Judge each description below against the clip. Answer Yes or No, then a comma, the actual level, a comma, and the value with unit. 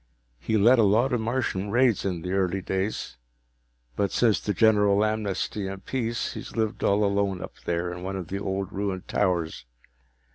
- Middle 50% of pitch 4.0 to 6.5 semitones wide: No, narrow, 2.5 semitones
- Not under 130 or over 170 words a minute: No, average, 180 wpm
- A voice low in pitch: Yes, low, 100 Hz